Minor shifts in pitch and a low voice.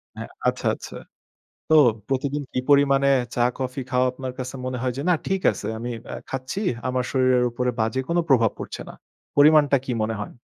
Yes: narrow, 1.9 semitones; low, 130 Hz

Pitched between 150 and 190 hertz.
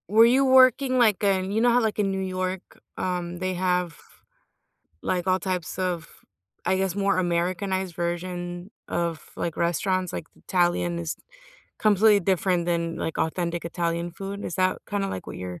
Yes: medium, 185 Hz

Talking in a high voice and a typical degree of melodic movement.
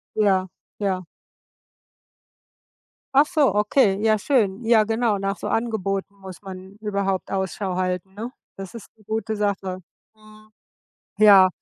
No: high, 200 Hz; narrow, 2.3 semitones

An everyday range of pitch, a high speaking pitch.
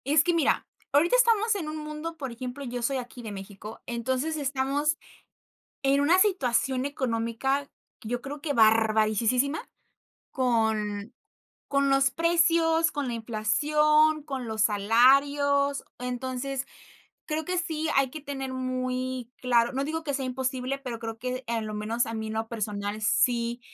Yes: average, 3.9 semitones; very high, 260 Hz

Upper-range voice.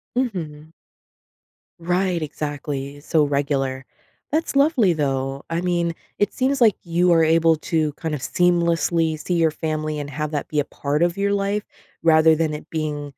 No: medium, 160 Hz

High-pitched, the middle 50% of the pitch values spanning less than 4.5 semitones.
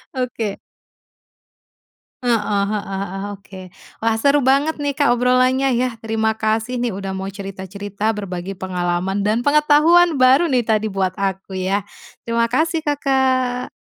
No: high, 225 Hz; average, 5.1 semitones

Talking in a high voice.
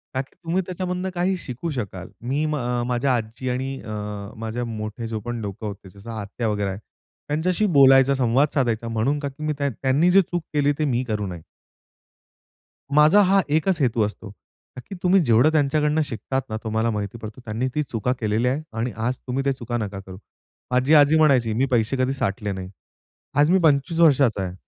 No: low, 125 Hz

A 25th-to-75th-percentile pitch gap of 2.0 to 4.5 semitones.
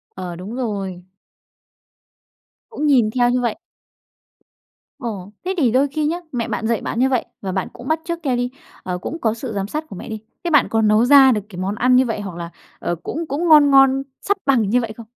No: average, 4.9 semitones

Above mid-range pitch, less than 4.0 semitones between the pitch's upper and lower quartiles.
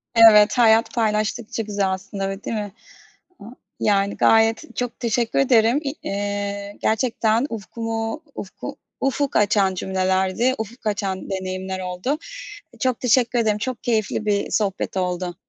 Yes: high, 215 Hz; average, 2.8 semitones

